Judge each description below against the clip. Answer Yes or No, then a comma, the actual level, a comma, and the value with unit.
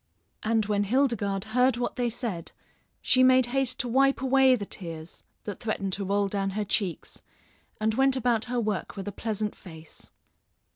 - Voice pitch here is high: Yes, high, 220 Hz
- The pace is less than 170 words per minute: No, average, 175 wpm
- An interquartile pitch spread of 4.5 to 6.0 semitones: No, average, 4.0 semitones